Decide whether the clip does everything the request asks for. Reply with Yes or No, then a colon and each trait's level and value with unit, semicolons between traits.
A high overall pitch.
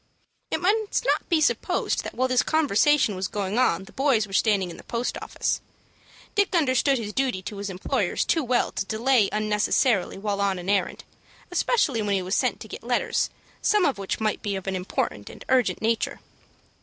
Yes: high, 220 Hz